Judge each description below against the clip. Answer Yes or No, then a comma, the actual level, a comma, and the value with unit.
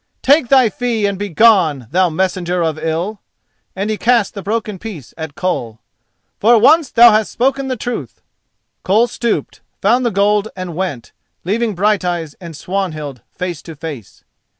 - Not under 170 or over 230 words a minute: No, average, 155 wpm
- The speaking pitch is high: Yes, high, 195 Hz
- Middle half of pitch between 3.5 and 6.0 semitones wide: Yes, average, 5.3 semitones